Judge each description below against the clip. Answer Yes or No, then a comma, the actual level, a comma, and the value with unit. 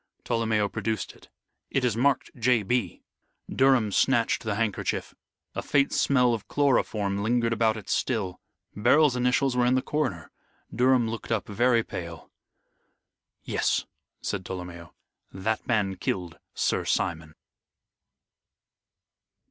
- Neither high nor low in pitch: No, low, 115 Hz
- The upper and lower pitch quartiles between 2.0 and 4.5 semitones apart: Yes, average, 3.9 semitones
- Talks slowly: Yes, slow, 125 wpm